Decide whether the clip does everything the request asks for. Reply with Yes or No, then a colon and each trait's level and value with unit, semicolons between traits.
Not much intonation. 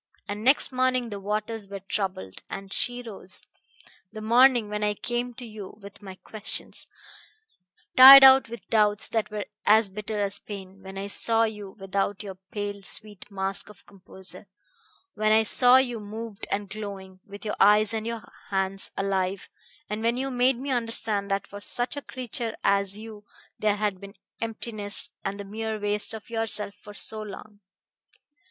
Yes: narrow, 2.3 semitones